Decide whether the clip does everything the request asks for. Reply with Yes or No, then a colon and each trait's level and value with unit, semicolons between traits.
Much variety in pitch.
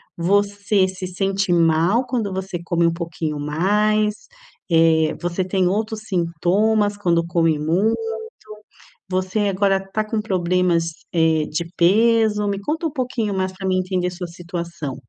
No: average, 3.4 semitones